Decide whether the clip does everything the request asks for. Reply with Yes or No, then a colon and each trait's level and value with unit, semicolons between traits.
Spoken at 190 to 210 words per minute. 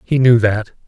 Yes: fast, 205 wpm